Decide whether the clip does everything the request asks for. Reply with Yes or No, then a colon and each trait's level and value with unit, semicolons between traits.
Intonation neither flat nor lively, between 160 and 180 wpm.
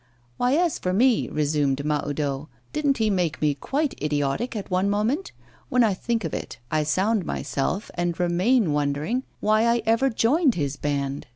No: wide, 8.0 semitones; average, 170 wpm